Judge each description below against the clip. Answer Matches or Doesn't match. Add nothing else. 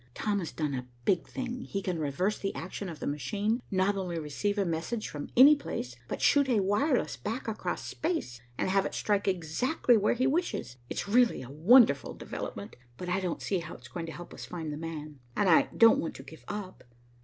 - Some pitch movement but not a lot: Doesn't match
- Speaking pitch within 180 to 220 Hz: Matches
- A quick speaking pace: Matches